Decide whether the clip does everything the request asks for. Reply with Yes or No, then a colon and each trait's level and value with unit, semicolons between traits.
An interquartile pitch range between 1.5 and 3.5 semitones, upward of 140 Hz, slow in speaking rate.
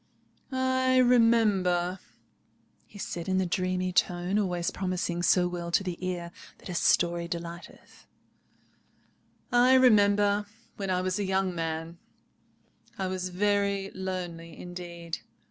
Yes: narrow, 2.5 semitones; medium, 185 Hz; slow, 120 wpm